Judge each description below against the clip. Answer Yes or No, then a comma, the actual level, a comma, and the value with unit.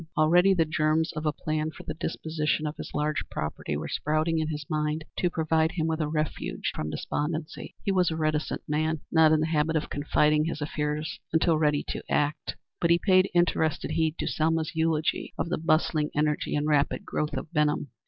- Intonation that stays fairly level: Yes, narrow, 1.1 semitones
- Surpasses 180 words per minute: Yes, average, 200 wpm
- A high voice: No, medium, 155 Hz